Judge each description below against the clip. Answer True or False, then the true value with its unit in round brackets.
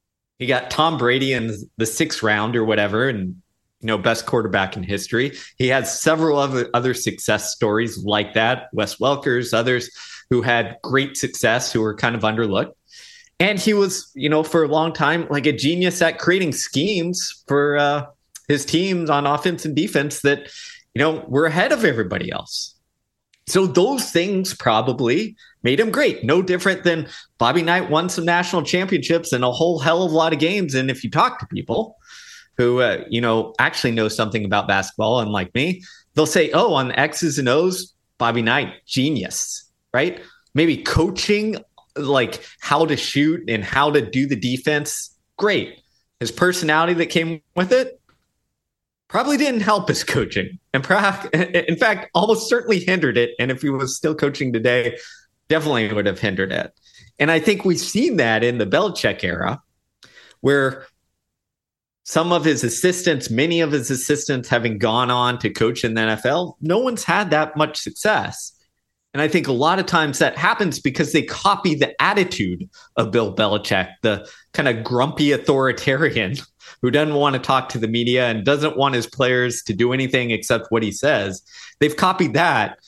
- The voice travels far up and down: True (6.0 semitones)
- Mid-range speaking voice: True (145 Hz)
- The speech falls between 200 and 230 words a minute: False (180 wpm)